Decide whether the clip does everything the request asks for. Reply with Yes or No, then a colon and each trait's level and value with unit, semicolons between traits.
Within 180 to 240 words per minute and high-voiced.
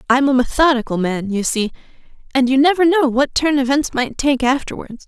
Yes: average, 200 wpm; very high, 265 Hz